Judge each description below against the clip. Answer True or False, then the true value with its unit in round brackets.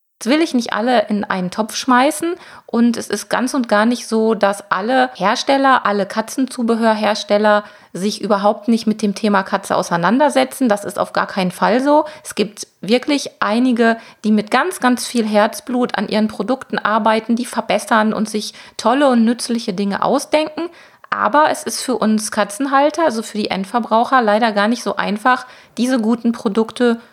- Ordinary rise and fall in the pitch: True (3.4 semitones)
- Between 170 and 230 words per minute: True (175 wpm)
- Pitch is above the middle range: True (225 Hz)